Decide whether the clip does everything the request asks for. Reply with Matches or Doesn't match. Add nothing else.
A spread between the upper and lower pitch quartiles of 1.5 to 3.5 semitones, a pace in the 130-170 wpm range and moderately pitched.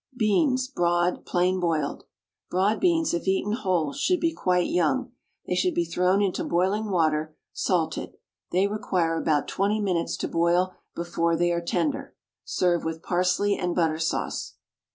Matches